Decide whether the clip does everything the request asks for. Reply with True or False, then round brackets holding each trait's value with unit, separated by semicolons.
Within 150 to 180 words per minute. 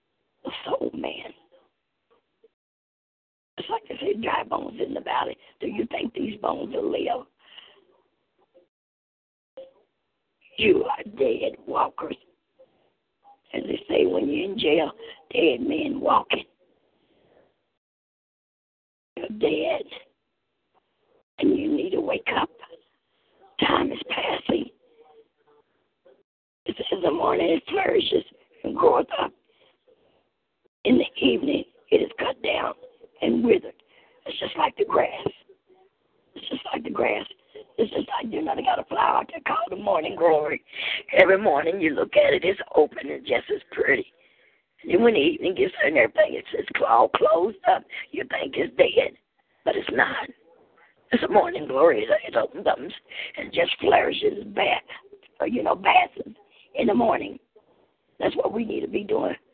False (140 wpm)